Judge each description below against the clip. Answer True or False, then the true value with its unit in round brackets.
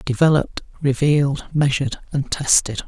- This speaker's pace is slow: True (105 wpm)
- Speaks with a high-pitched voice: False (140 Hz)